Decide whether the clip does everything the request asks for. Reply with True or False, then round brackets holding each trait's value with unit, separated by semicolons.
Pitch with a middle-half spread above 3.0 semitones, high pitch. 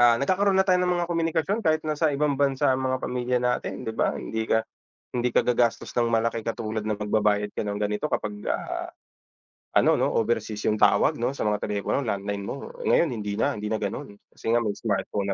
False (4.8 semitones; 115 Hz)